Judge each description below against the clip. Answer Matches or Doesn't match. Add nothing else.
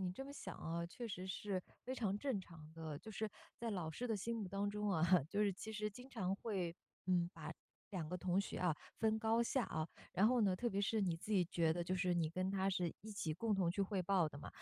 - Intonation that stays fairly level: Doesn't match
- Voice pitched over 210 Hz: Doesn't match